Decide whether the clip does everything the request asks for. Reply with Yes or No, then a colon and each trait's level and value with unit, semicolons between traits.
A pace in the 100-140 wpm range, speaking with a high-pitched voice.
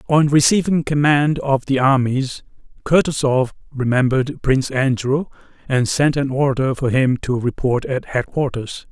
No: slow, 135 wpm; low, 135 Hz